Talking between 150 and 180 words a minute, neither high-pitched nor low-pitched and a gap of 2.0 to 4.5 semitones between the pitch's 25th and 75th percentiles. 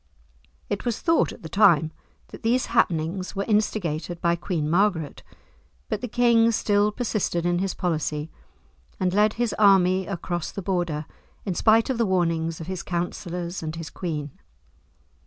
Yes: average, 155 wpm; medium, 180 Hz; average, 4.0 semitones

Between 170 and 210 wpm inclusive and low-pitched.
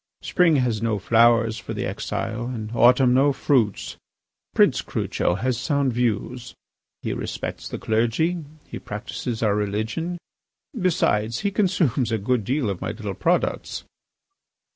No: average, 140 wpm; low, 120 Hz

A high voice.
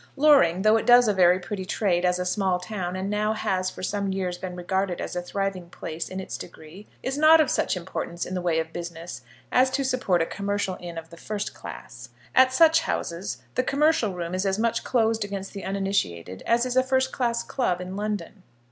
Yes: high, 195 Hz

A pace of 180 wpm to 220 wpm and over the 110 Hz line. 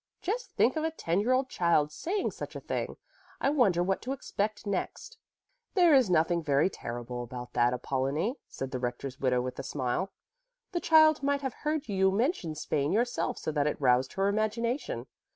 Yes: average, 190 wpm; high, 190 Hz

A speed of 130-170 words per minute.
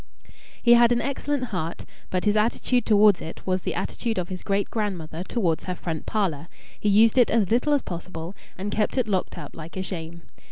No: fast, 205 wpm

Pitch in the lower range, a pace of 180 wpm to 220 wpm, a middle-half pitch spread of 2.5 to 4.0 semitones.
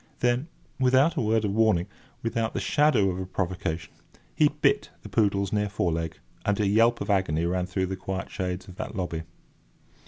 Yes: low, 100 Hz; average, 190 wpm; average, 3.5 semitones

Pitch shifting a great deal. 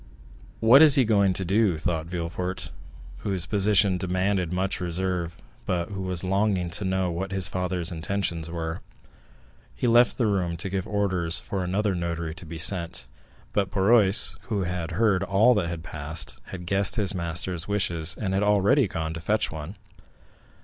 No: average, 2.8 semitones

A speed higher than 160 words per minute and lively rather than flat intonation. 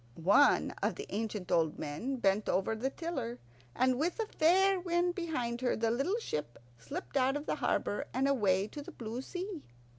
Yes: average, 185 wpm; wide, 7.6 semitones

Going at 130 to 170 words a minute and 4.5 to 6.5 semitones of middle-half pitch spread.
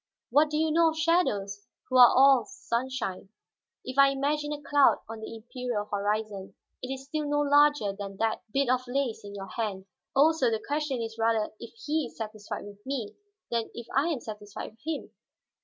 No: average, 190 wpm; average, 5.3 semitones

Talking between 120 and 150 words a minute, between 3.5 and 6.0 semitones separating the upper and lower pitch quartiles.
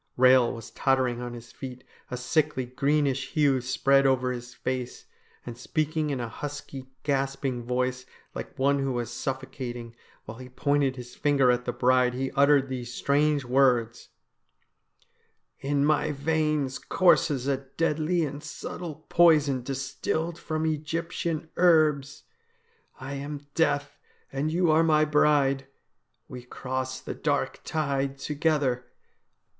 No: slow, 135 wpm; average, 2.9 semitones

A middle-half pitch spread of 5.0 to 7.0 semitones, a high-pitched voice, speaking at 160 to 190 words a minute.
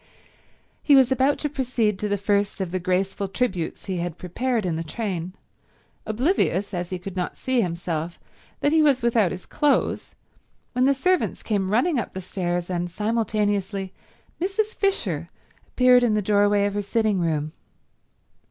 Yes: wide, 5.4 semitones; high, 205 Hz; average, 165 wpm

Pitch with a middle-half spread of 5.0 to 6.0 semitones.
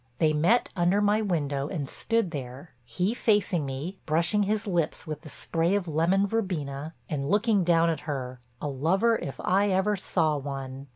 Yes: wide, 5.6 semitones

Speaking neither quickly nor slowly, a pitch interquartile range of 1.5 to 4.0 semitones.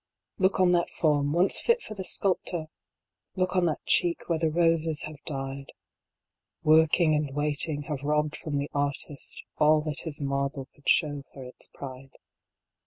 Yes: average, 175 wpm; average, 2.8 semitones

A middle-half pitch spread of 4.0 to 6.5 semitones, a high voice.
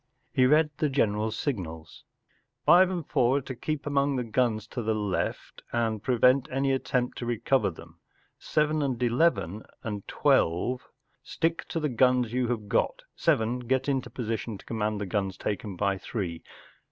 No: average, 4.4 semitones; low, 120 Hz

